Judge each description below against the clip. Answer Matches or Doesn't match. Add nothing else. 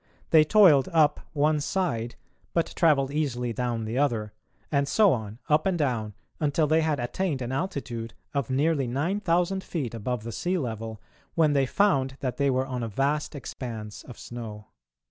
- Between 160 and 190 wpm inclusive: Matches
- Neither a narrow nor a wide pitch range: Matches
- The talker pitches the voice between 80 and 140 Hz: Matches